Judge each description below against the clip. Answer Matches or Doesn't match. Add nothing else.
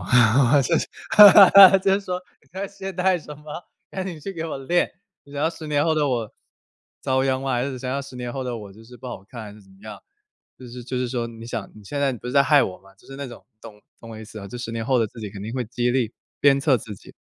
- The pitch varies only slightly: Doesn't match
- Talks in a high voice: Doesn't match